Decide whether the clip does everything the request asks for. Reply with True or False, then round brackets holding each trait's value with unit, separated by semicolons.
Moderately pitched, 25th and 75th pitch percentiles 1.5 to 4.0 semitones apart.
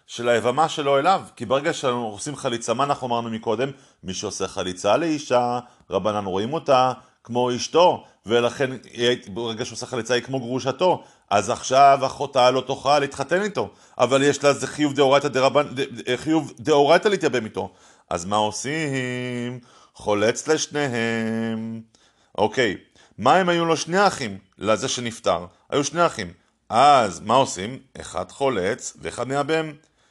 False (130 Hz; 3.7 semitones)